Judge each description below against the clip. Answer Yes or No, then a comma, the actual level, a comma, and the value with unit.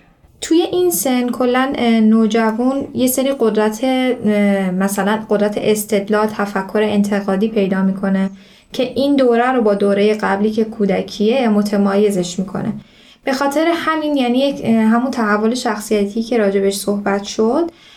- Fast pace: No, average, 125 wpm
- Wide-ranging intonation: No, average, 3.8 semitones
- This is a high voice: Yes, high, 220 Hz